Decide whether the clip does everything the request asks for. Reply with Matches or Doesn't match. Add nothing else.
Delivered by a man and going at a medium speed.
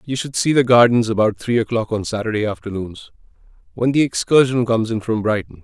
Matches